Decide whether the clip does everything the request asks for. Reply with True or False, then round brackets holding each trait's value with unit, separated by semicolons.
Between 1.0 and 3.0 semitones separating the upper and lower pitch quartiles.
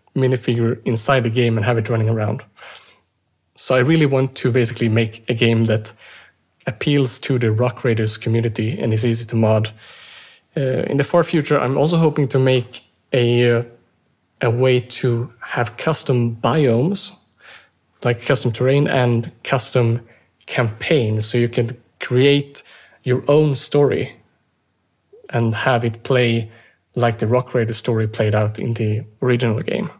True (2.4 semitones)